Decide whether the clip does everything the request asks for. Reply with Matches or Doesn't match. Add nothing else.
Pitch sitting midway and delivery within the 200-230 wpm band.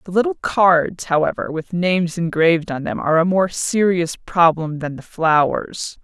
Doesn't match